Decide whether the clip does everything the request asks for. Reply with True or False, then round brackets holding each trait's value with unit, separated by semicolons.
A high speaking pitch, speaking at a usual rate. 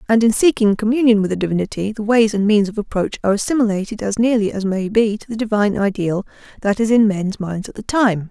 False (210 Hz; 230 wpm)